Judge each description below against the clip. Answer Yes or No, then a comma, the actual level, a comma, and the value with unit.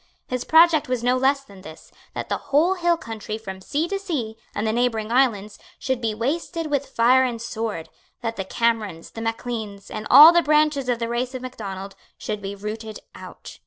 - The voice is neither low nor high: No, high, 235 Hz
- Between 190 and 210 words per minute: Yes, average, 200 wpm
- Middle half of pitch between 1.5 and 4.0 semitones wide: No, average, 4.5 semitones